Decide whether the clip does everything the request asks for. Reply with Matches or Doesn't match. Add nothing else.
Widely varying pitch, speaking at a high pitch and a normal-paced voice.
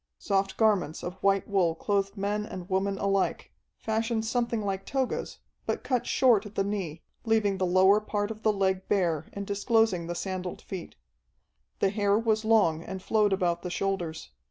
Doesn't match